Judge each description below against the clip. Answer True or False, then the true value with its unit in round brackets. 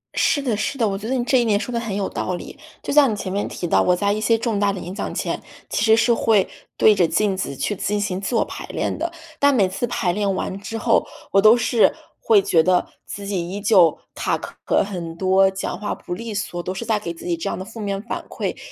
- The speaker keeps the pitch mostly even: False (3.1 semitones)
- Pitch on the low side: False (205 Hz)